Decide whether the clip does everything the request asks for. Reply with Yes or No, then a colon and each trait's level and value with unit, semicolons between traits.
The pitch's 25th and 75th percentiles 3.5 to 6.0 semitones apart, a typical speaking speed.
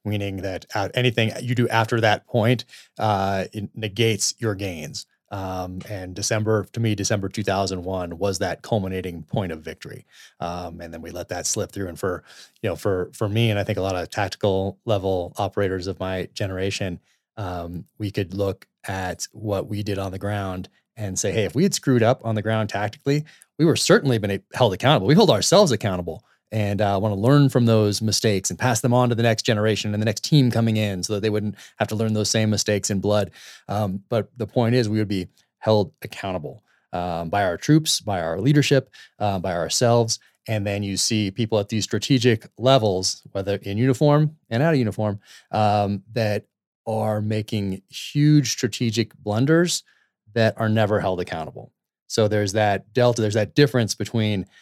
No: average, 2.9 semitones; average, 195 wpm